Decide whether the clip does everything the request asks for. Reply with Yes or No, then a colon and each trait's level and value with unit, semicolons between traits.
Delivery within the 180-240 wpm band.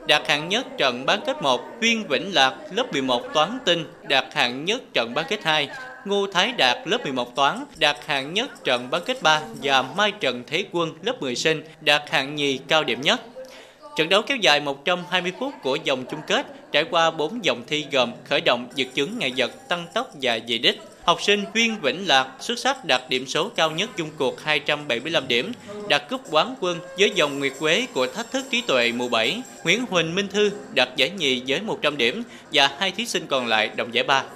Yes: average, 220 wpm